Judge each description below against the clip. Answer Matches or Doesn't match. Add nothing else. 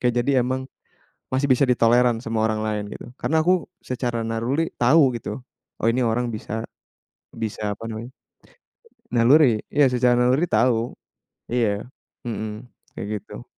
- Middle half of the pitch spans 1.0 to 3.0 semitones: Matches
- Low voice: Matches